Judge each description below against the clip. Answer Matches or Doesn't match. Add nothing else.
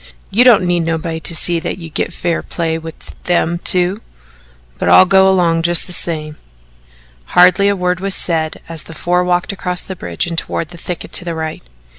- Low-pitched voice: Doesn't match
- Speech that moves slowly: Doesn't match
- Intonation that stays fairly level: Matches